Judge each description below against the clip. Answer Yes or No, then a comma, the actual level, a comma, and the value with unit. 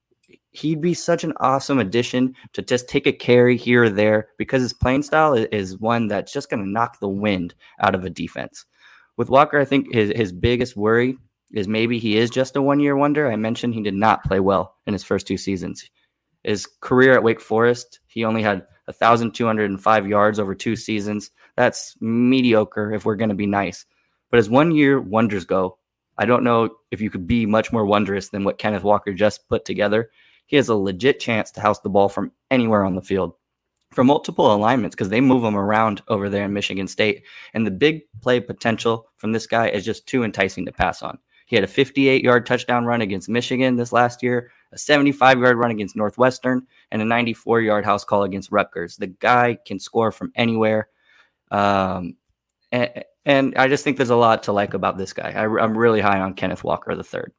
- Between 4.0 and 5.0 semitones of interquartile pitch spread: No, average, 3.3 semitones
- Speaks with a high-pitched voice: No, low, 115 Hz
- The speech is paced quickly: Yes, fast, 210 wpm